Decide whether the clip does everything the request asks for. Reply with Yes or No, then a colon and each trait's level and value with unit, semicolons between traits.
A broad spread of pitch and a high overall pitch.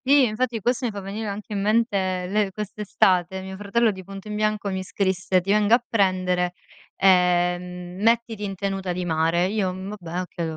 No: narrow, 2.6 semitones; high, 195 Hz